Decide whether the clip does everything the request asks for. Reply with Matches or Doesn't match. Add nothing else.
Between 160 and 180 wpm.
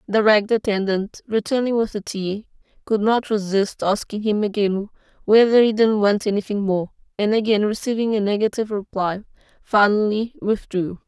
Doesn't match